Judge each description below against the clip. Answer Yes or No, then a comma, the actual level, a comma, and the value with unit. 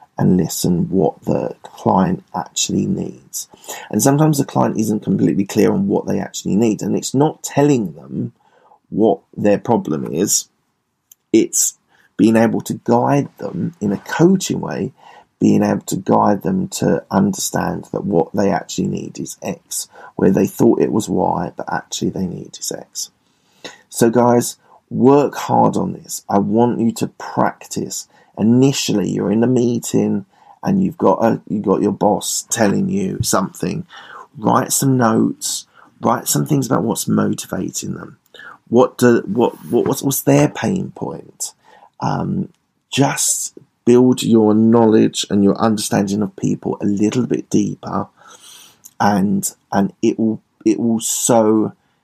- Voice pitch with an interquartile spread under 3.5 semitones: No, average, 4.2 semitones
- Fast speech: No, average, 150 wpm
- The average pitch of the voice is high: No, low, 115 Hz